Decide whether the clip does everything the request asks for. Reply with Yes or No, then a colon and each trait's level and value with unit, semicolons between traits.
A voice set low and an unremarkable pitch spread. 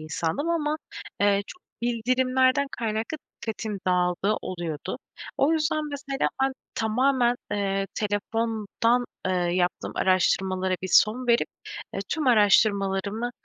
No: high, 220 Hz; average, 4.8 semitones